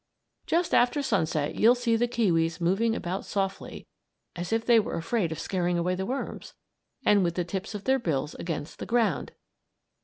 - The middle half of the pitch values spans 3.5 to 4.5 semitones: No, average, 5.2 semitones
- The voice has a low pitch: No, high, 195 Hz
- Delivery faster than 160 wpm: Yes, average, 180 wpm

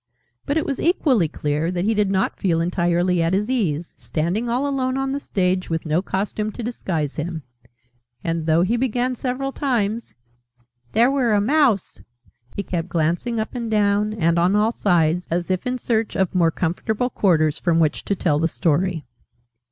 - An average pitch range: No, wide, 5.9 semitones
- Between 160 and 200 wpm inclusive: Yes, average, 185 wpm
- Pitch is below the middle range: No, high, 190 Hz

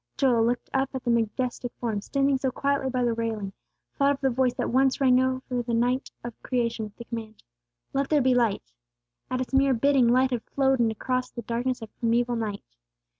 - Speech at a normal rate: No, fast, 215 wpm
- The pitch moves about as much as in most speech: No, narrow, 2.2 semitones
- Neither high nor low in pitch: No, high, 245 Hz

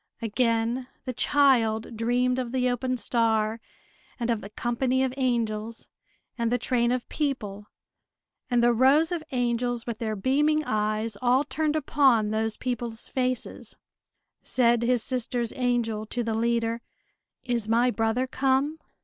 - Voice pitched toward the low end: No, high, 240 Hz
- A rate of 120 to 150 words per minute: Yes, average, 140 wpm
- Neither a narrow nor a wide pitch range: No, narrow, 2.3 semitones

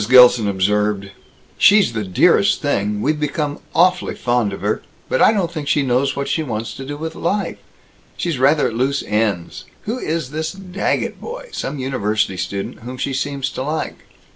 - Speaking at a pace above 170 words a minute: Yes, average, 180 wpm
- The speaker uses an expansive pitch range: Yes, wide, 6.6 semitones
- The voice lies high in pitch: No, low, 135 Hz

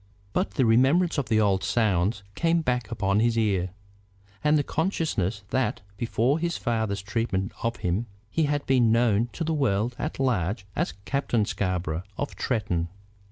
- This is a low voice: Yes, low, 115 Hz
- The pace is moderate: Yes, average, 160 wpm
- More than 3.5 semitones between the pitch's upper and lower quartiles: Yes, wide, 5.5 semitones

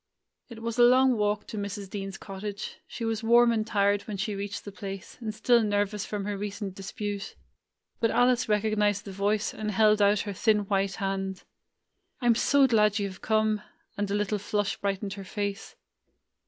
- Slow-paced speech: No, average, 195 wpm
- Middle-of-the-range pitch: No, high, 205 Hz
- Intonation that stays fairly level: Yes, narrow, 1.6 semitones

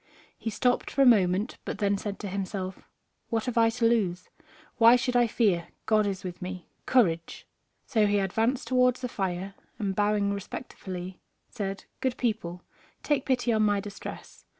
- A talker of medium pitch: No, high, 210 Hz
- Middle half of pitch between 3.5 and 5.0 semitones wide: Yes, average, 3.8 semitones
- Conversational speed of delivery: Yes, average, 170 wpm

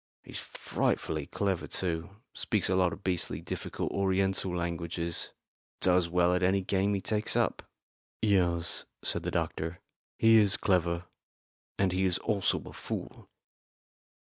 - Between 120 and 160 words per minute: Yes, average, 140 wpm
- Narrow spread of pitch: Yes, narrow, 2.1 semitones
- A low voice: Yes, very low, 90 Hz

